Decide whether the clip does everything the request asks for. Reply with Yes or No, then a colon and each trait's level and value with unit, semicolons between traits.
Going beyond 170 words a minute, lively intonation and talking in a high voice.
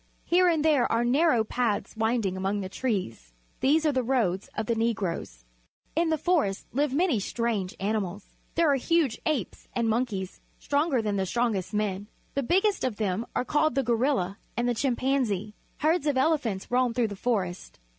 Yes: average, 185 wpm; wide, 5.7 semitones; high, 235 Hz